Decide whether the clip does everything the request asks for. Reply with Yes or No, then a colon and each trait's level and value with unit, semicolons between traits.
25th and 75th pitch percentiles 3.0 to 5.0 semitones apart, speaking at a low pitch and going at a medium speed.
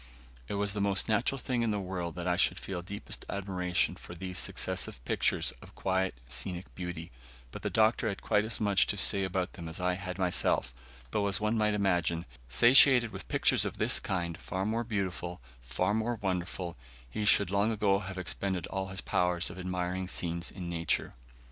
No: narrow, 2.6 semitones; very low, 95 Hz; average, 190 wpm